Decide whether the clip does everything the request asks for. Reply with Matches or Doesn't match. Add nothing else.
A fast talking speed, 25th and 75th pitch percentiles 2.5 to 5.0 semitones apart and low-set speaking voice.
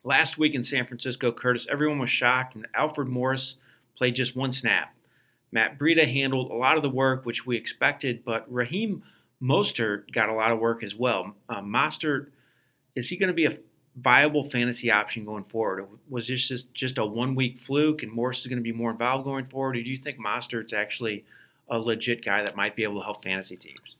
Matches